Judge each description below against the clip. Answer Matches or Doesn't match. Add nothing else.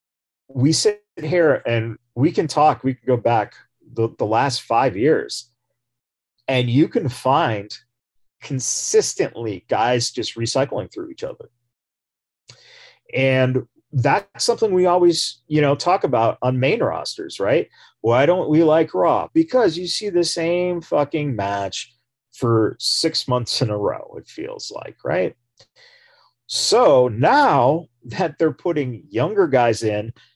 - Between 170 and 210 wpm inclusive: Doesn't match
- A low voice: Matches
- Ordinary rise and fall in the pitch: Doesn't match